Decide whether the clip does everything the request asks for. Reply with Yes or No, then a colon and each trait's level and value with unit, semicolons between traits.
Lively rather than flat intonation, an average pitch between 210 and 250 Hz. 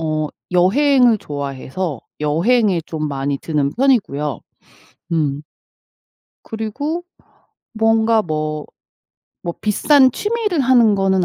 No: wide, 8.0 semitones; high, 190 Hz